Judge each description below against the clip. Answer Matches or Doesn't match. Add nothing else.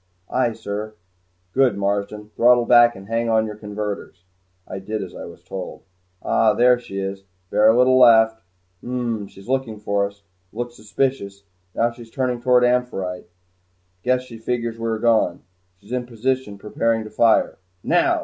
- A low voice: Matches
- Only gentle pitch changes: Doesn't match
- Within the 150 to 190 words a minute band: Matches